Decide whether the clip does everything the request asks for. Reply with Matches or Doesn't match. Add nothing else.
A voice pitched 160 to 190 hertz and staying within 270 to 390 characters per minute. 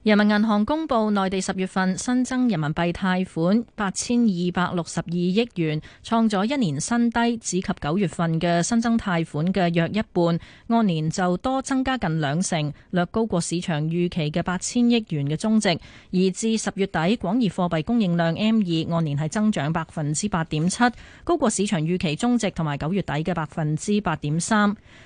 Matches